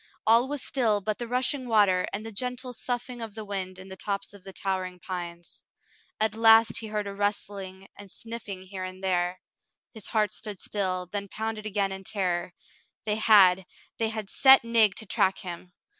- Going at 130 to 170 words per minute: No, average, 190 wpm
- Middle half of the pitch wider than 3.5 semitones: No, average, 2.9 semitones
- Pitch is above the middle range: Yes, high, 205 Hz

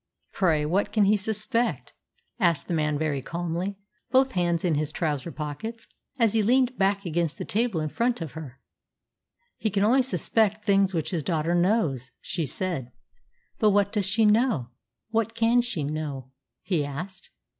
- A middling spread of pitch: No, wide, 5.9 semitones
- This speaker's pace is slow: No, average, 165 wpm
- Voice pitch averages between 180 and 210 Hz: Yes, medium, 185 Hz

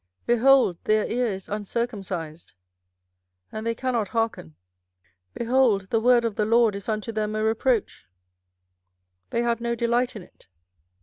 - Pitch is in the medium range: No, high, 225 Hz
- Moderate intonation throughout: No, narrow, 2.2 semitones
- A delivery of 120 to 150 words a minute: Yes, average, 140 wpm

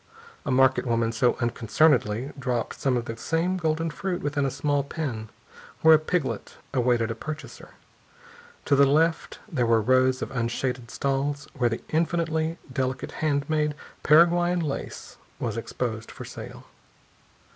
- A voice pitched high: No, low, 135 Hz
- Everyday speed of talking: Yes, average, 145 wpm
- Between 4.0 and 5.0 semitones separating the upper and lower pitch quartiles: Yes, average, 4.6 semitones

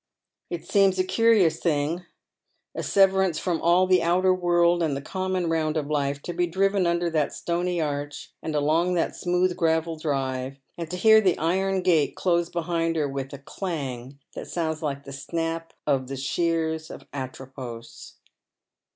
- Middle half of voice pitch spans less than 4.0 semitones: Yes, average, 3.6 semitones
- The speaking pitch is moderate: Yes, medium, 165 Hz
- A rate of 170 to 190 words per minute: Yes, average, 175 wpm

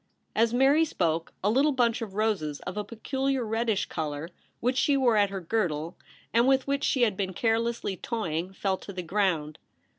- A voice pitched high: Yes, high, 215 Hz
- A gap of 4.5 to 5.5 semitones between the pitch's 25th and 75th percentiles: Yes, average, 5.0 semitones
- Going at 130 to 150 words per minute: No, average, 190 wpm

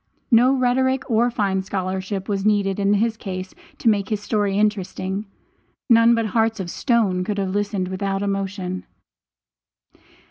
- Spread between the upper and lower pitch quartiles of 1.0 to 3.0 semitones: Yes, narrow, 2.6 semitones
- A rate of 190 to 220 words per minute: No, average, 145 wpm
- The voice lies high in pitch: Yes, high, 200 Hz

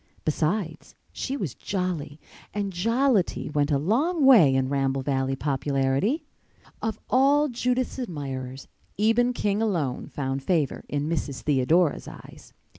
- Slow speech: Yes, slow, 125 wpm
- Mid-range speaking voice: Yes, medium, 165 Hz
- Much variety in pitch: Yes, wide, 8.5 semitones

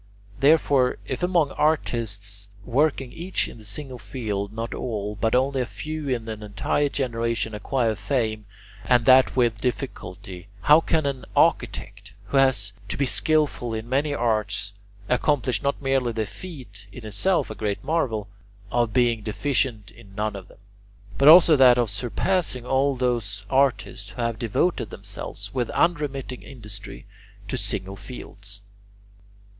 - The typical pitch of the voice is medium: No, low, 120 Hz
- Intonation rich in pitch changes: No, average, 4.5 semitones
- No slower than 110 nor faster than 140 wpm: No, average, 150 wpm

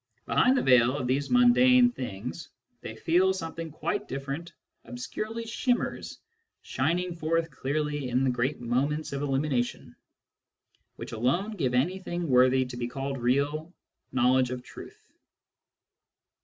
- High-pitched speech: No, medium, 140 Hz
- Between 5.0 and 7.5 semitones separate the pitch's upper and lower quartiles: Yes, wide, 5.4 semitones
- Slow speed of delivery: Yes, slow, 130 wpm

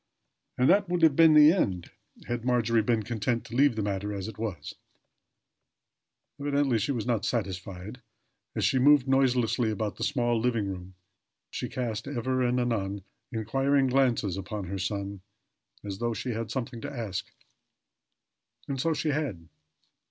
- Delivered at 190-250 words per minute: No, average, 160 wpm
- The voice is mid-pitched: No, low, 115 Hz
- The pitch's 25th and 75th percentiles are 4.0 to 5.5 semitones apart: Yes, average, 4.6 semitones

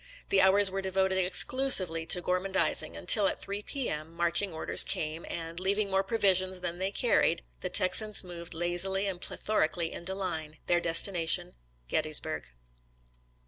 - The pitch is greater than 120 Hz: Yes, medium, 185 Hz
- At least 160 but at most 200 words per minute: No, average, 150 wpm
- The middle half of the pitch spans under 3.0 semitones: Yes, narrow, 2.5 semitones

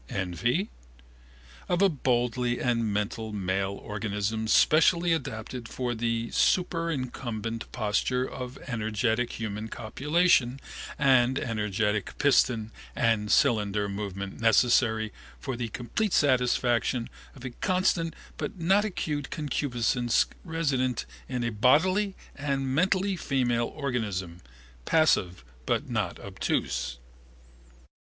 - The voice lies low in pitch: Yes, low, 120 Hz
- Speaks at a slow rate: Yes, slow, 100 wpm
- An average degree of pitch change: Yes, average, 4.7 semitones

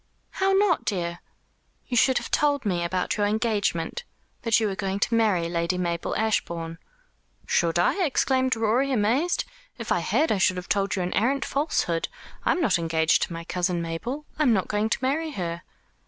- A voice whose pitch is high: Yes, high, 205 Hz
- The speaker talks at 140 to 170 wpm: No, average, 190 wpm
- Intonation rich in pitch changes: Yes, wide, 7.1 semitones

